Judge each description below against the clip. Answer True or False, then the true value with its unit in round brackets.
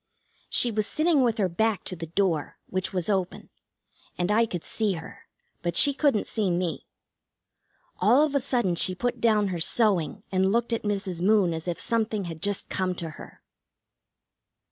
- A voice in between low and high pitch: False (195 Hz)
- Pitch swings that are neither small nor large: True (4.2 semitones)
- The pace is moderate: True (180 wpm)